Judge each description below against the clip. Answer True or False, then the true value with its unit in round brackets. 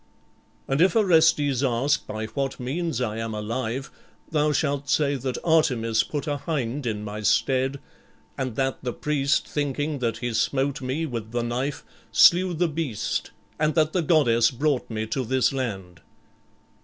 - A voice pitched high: False (135 Hz)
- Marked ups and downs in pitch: False (4.1 semitones)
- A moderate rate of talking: True (165 wpm)